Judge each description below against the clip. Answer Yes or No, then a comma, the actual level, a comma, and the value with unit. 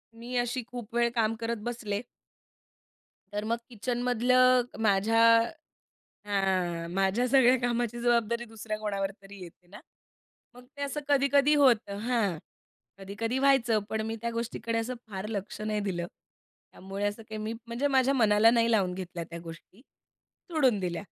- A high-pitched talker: Yes, high, 225 Hz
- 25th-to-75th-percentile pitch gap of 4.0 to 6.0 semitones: No, average, 3.4 semitones